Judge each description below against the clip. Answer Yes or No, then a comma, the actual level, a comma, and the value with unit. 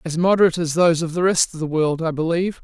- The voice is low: No, medium, 165 Hz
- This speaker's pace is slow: No, fast, 275 wpm